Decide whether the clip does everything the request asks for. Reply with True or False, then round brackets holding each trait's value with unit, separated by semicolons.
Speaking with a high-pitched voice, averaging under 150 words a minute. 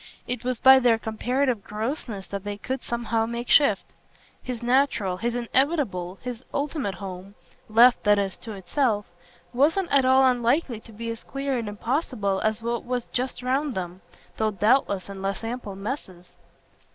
False (235 Hz; 165 wpm)